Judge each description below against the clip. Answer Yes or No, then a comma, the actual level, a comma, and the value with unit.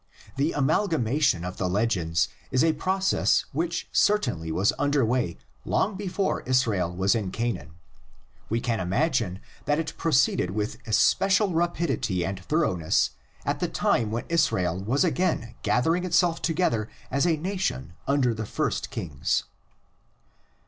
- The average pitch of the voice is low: Yes, low, 125 Hz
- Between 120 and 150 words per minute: Yes, average, 140 wpm